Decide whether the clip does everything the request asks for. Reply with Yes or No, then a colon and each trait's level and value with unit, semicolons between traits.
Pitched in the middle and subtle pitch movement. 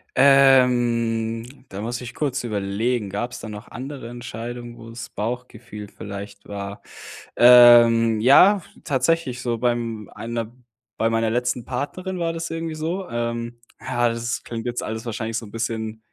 No: low, 120 Hz; narrow, 1.8 semitones